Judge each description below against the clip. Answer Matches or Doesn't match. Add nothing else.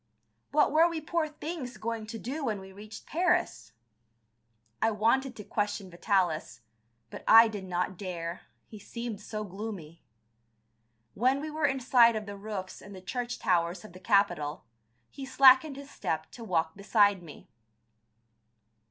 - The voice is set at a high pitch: Matches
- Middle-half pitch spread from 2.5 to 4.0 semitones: Doesn't match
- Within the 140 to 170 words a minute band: Matches